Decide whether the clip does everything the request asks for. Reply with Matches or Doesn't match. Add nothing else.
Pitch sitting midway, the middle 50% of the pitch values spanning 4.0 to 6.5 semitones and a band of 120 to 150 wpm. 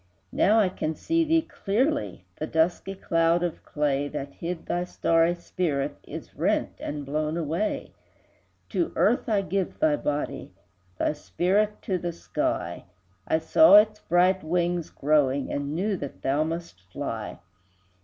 Matches